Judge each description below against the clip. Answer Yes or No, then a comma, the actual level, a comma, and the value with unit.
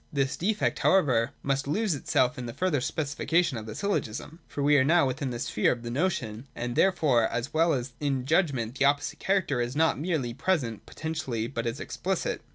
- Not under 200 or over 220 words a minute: Yes, fast, 205 wpm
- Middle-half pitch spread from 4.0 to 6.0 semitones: Yes, average, 4.9 semitones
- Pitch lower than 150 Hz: Yes, medium, 140 Hz